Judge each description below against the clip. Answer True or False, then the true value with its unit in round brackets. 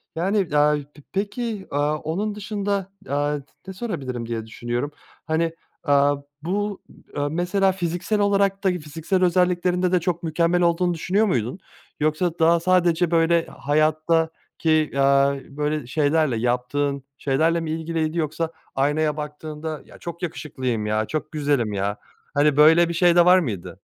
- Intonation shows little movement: False (3.6 semitones)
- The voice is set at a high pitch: False (160 Hz)